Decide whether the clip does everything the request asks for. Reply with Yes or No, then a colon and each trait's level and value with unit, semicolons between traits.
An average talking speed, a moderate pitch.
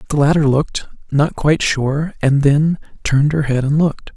Yes: average, 190 wpm; medium, 145 Hz